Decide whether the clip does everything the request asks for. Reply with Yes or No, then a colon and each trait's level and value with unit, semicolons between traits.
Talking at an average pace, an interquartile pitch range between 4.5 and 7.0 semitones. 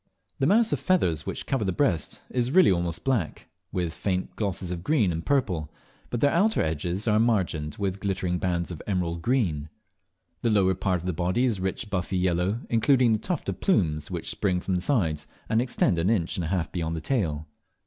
No: fast, 210 wpm; average, 5.3 semitones